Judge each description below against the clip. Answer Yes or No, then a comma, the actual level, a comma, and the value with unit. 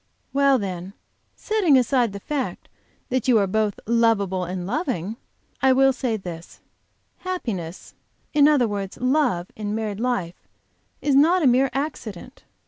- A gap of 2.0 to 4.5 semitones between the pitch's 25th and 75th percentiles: No, wide, 5.5 semitones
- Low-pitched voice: No, high, 235 Hz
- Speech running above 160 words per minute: No, average, 140 wpm